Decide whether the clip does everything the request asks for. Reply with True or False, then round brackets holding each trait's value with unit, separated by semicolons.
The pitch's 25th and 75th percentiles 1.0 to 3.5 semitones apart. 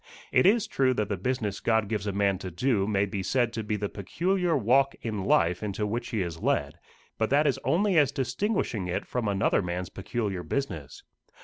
False (5.2 semitones)